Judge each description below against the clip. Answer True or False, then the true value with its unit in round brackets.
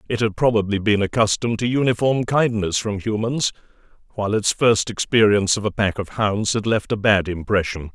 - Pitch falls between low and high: False (105 Hz)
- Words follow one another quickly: False (180 wpm)